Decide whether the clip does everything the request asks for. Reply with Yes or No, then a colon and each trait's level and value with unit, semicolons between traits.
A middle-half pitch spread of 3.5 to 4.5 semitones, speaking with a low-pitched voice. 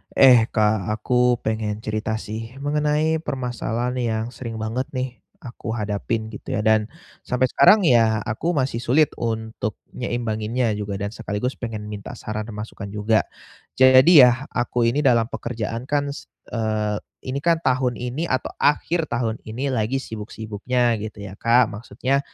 No: average, 3.0 semitones; low, 115 Hz